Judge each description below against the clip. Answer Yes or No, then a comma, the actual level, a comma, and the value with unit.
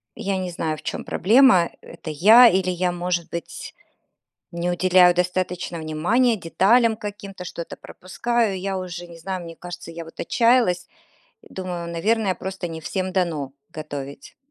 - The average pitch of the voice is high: No, medium, 180 Hz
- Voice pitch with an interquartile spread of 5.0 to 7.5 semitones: No, narrow, 2.4 semitones